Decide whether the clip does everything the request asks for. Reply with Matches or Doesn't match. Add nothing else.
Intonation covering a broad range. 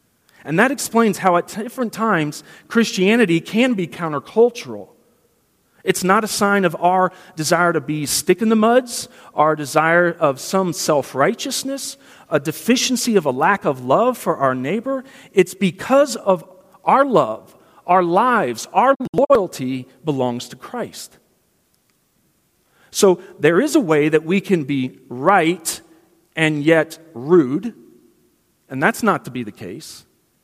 Matches